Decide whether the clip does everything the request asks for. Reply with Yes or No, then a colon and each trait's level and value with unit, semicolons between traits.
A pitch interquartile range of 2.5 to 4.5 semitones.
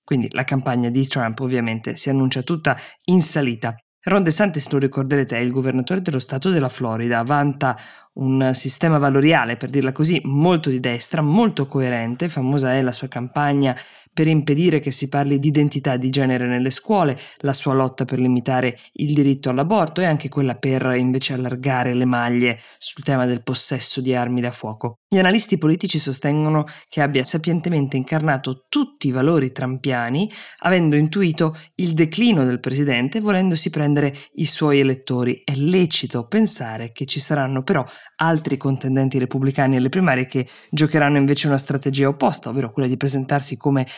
Yes: average, 3.0 semitones